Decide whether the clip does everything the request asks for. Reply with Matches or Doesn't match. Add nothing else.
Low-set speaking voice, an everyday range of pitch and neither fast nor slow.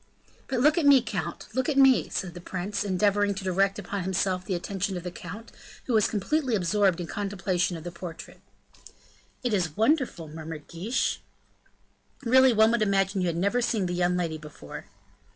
Doesn't match